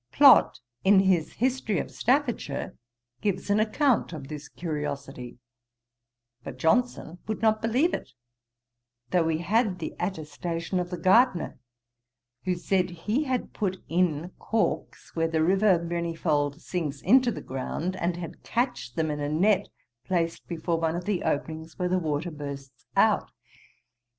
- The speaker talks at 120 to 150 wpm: Yes, average, 145 wpm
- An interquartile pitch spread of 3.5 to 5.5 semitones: Yes, average, 4.7 semitones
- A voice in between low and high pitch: Yes, medium, 175 Hz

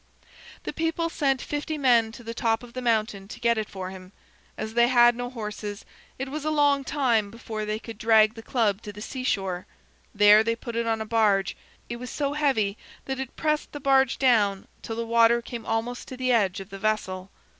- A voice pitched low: No, high, 230 Hz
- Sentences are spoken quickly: Yes, fast, 215 wpm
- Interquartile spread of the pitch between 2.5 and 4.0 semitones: Yes, average, 3.3 semitones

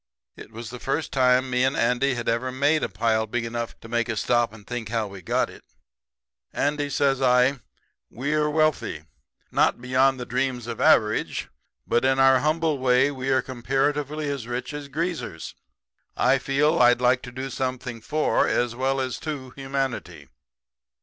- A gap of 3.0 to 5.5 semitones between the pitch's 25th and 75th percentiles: No, narrow, 2.4 semitones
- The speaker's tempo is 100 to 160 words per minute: No, average, 180 wpm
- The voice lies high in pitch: No, low, 130 Hz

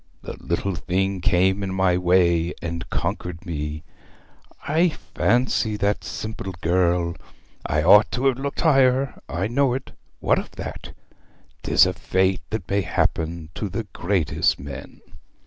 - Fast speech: No, average, 145 wpm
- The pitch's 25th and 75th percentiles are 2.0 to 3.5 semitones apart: No, average, 4.4 semitones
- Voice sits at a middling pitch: No, very low, 95 Hz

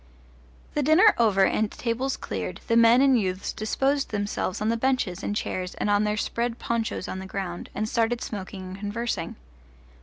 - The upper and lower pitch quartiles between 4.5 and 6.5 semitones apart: No, average, 3.4 semitones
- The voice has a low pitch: No, high, 215 Hz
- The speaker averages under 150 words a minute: No, average, 180 wpm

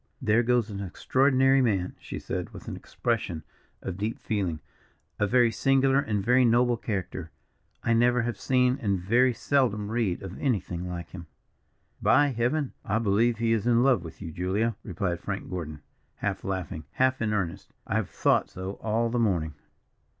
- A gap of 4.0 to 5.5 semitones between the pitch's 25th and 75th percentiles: Yes, average, 4.7 semitones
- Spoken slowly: No, average, 170 wpm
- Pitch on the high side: No, low, 110 Hz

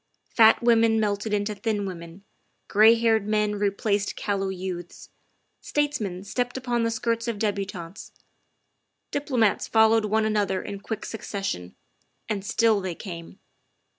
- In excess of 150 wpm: No, average, 140 wpm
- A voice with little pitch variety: Yes, narrow, 2.3 semitones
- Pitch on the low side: No, high, 210 Hz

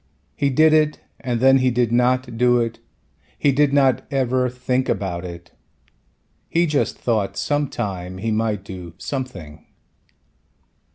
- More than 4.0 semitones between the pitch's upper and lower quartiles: Yes, average, 4.8 semitones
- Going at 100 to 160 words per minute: Yes, average, 145 wpm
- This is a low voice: Yes, low, 125 Hz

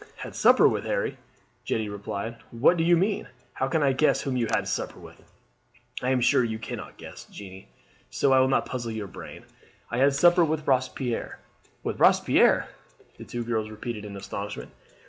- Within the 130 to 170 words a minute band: No, average, 185 wpm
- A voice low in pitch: Yes, low, 125 Hz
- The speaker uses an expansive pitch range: No, average, 4.1 semitones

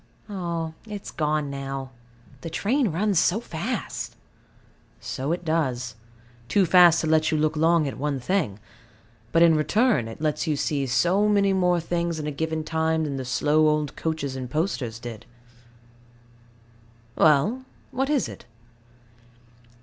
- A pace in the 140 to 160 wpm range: Yes, average, 150 wpm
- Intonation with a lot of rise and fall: No, average, 3.8 semitones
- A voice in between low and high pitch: Yes, medium, 160 Hz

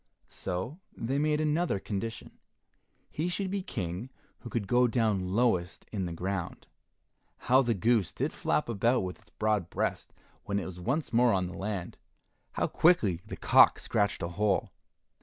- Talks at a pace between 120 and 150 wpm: No, average, 165 wpm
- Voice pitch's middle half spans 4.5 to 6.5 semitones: Yes, average, 4.9 semitones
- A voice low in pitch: Yes, low, 110 Hz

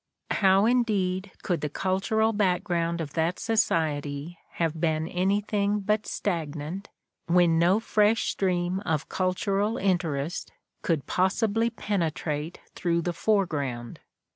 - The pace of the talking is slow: Yes, slow, 115 wpm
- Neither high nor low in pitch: Yes, medium, 180 Hz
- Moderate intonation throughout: Yes, average, 3.8 semitones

